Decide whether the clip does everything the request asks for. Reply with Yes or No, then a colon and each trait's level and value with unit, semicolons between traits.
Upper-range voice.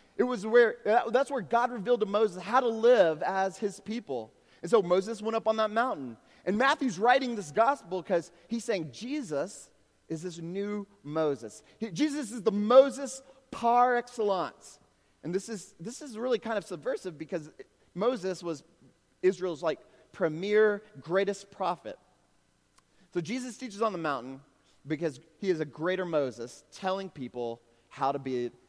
Yes: high, 195 Hz